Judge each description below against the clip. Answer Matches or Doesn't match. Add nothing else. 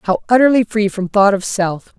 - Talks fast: Matches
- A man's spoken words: Doesn't match